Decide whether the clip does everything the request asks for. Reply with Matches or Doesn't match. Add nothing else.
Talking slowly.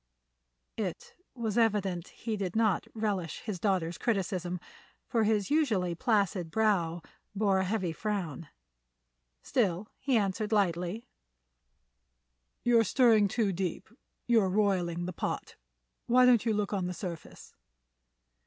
Matches